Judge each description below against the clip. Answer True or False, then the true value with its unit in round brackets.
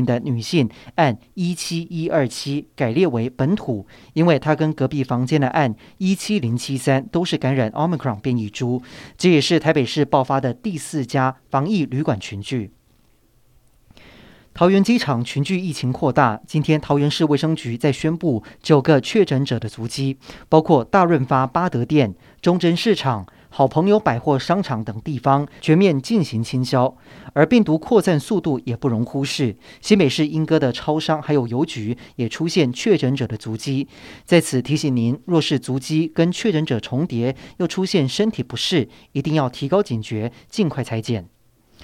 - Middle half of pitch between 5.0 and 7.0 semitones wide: False (4.6 semitones)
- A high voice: False (140 Hz)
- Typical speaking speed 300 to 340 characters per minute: False (260 characters per minute)